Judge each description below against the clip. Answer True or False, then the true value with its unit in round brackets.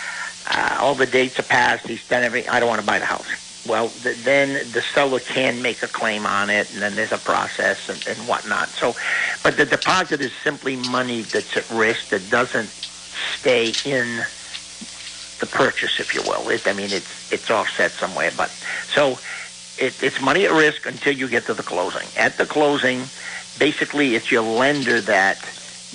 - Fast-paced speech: False (190 wpm)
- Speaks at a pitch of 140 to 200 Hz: False (125 Hz)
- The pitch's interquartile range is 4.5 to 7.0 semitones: True (5.5 semitones)